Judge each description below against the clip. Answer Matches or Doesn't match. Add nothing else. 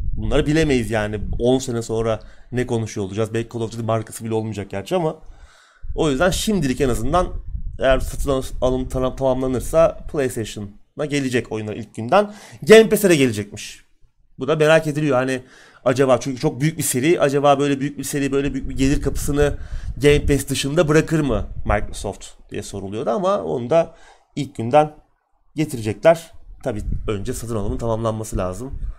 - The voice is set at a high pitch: Doesn't match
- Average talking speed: Doesn't match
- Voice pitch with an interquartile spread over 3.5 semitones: Matches